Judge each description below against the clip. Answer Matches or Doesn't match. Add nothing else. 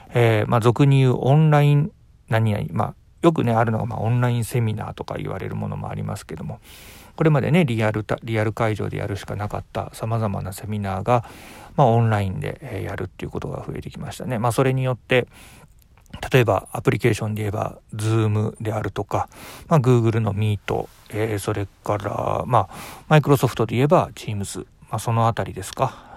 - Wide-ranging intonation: Doesn't match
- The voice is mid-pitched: Doesn't match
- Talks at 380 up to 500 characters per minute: Matches